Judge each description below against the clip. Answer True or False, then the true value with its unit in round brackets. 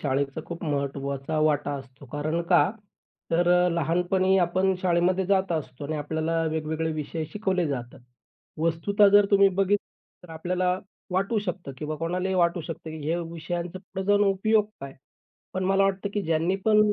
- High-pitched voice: False (175 Hz)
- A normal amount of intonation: True (3.5 semitones)